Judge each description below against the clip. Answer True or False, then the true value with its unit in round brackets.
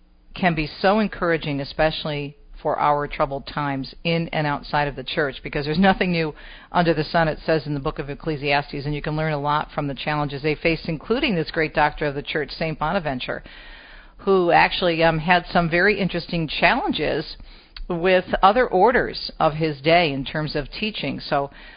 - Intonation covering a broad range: False (2.9 semitones)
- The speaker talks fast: False (185 wpm)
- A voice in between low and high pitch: True (155 Hz)